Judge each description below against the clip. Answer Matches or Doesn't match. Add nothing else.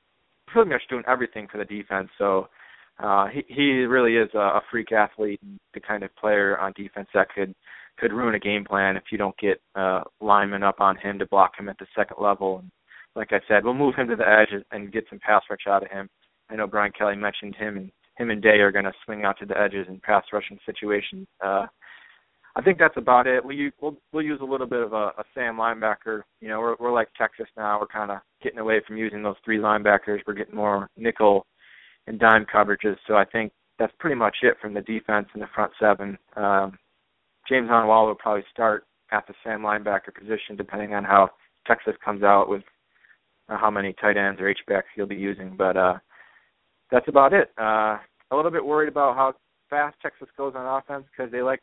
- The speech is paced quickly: Matches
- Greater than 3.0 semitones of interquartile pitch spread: Doesn't match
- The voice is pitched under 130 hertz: Matches